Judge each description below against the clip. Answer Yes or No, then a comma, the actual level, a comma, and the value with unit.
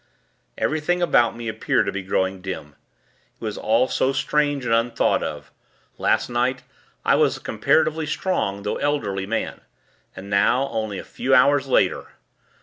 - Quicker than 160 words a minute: No, average, 155 wpm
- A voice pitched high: No, low, 120 Hz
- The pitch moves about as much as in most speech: No, wide, 5.9 semitones